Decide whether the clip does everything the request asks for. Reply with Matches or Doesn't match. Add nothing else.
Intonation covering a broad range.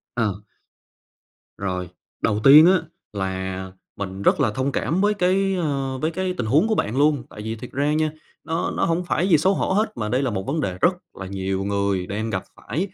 Matches